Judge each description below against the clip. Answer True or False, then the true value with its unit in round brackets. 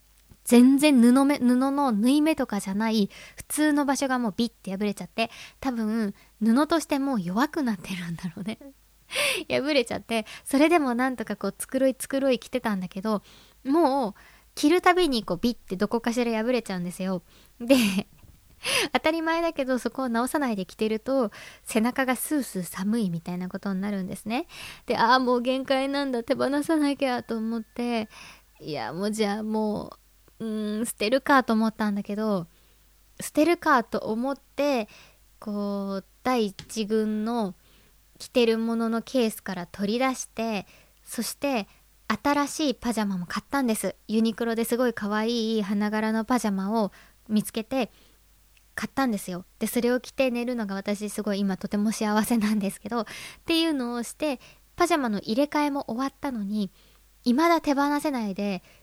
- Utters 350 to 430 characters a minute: False (335 characters per minute)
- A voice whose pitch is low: False (230 Hz)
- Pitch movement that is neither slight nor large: True (4.3 semitones)